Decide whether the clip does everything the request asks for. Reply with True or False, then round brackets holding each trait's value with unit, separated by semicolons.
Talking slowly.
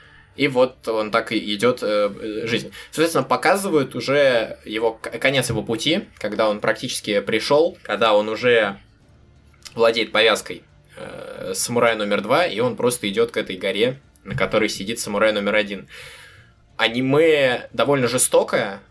False (145 wpm)